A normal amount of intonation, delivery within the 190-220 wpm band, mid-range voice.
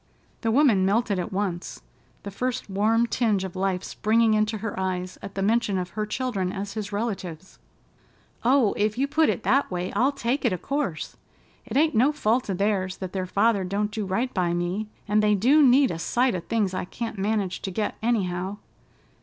No: average, 3.7 semitones; average, 200 wpm; high, 210 Hz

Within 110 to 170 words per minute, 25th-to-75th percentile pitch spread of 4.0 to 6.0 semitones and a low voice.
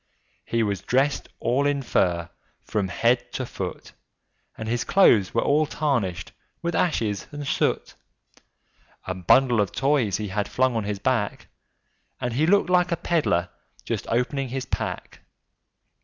Yes: average, 155 wpm; wide, 5.6 semitones; low, 120 Hz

